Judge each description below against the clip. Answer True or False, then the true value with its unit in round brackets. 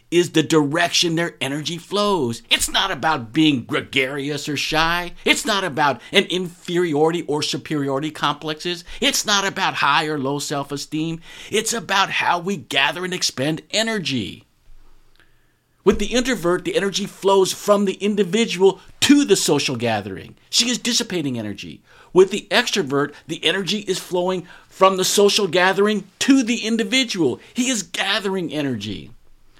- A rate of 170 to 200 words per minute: False (145 wpm)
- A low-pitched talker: False (175 Hz)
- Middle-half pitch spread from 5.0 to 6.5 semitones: True (5.4 semitones)